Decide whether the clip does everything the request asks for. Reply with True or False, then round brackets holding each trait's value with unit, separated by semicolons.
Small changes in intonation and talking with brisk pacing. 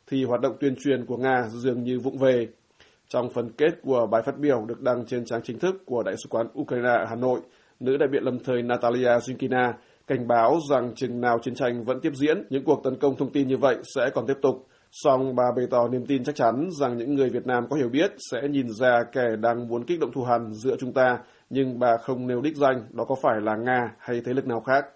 True (2.0 semitones; 255 wpm)